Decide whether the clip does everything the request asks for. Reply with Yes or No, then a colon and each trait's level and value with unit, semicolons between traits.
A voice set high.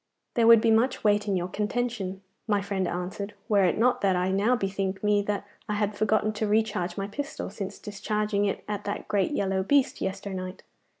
Yes: high, 205 Hz